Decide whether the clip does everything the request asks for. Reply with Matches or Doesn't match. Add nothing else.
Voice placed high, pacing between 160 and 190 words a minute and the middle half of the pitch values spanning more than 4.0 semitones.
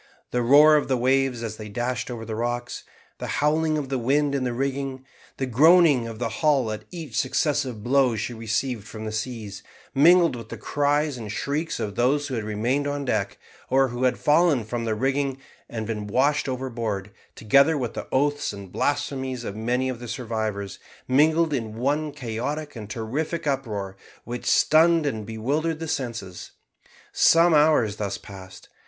Doesn't match